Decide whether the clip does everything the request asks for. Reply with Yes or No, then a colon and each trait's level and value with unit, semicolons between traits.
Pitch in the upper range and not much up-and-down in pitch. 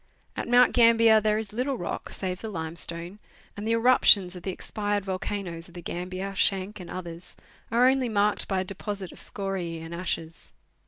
No: high, 195 Hz; average, 3.5 semitones